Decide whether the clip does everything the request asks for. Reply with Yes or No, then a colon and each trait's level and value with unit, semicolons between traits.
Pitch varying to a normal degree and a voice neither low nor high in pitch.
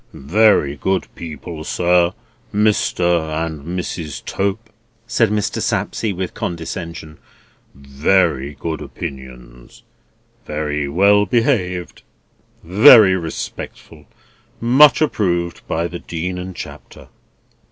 No: average, 4.4 semitones; very low, 85 Hz